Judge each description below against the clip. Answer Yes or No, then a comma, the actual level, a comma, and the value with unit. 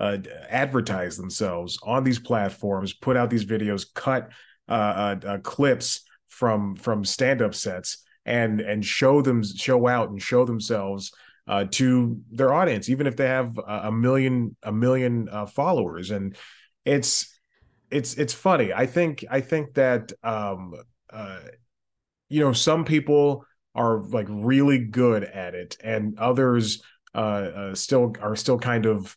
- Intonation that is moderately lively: Yes, average, 4.1 semitones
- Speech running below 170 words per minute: Yes, average, 150 wpm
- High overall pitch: No, low, 115 Hz